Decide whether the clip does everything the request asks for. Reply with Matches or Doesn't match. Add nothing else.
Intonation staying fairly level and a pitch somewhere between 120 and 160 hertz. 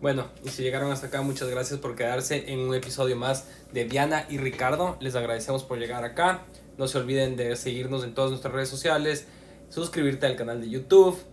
Matches